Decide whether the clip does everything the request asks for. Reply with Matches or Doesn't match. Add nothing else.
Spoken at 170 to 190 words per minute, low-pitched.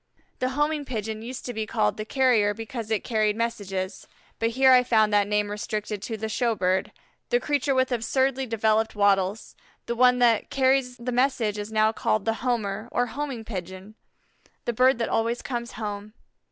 Doesn't match